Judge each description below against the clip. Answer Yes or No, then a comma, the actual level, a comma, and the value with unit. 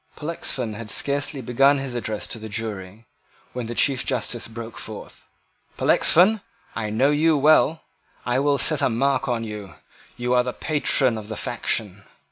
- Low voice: Yes, low, 125 Hz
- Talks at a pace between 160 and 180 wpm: Yes, average, 165 wpm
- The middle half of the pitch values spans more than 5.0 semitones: No, average, 4.1 semitones